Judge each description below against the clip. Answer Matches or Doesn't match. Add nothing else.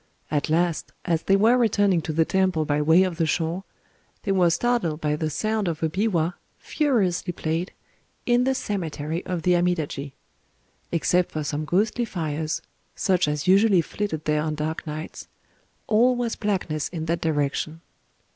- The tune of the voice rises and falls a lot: Doesn't match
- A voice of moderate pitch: Matches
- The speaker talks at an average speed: Matches